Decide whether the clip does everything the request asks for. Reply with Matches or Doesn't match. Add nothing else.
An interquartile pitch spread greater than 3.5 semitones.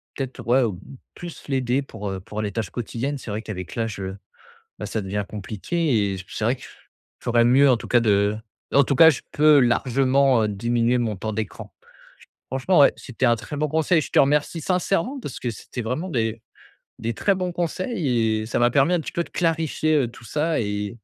Matches